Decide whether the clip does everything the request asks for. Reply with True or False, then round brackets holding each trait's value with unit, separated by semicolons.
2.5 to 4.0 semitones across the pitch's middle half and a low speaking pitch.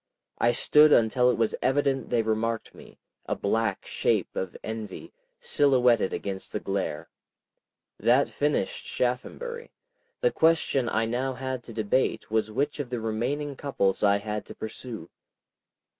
True (3.7 semitones; 120 Hz)